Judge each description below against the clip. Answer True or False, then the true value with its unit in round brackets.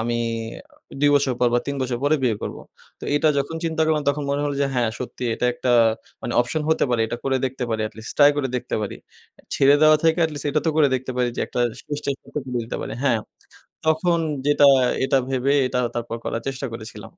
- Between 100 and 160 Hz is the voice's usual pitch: True (135 Hz)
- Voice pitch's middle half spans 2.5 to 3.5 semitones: True (3.2 semitones)